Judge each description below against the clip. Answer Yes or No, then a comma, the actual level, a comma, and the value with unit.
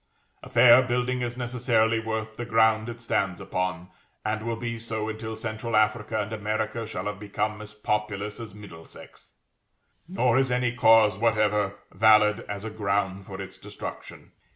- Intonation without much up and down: Yes, narrow, 1.7 semitones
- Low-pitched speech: Yes, low, 110 Hz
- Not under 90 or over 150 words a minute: No, average, 160 wpm